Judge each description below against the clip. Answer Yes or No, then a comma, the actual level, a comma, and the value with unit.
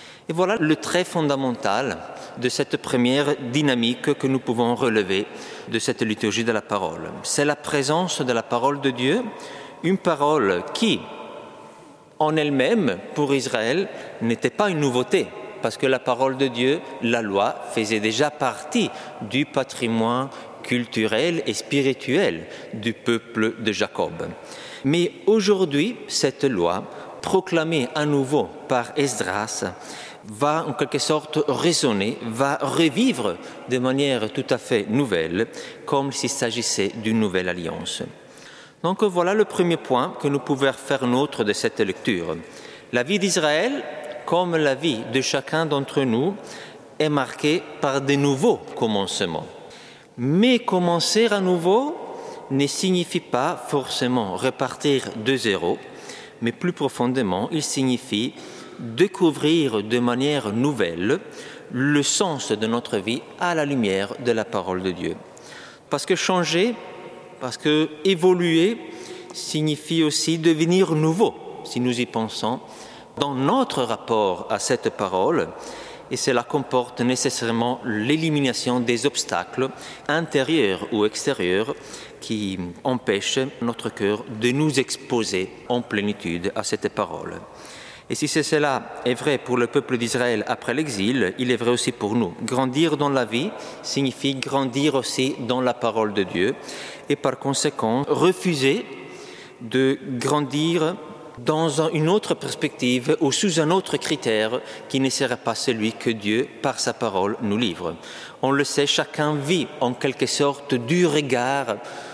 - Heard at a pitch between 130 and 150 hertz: Yes, medium, 140 Hz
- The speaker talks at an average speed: No, slow, 140 wpm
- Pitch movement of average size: Yes, average, 4.2 semitones